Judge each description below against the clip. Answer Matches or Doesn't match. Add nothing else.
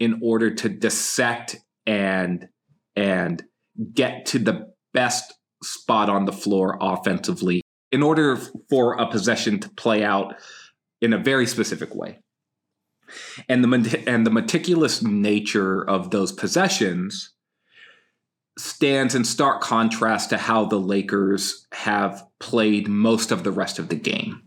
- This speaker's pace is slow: Matches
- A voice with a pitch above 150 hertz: Doesn't match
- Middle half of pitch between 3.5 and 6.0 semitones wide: Matches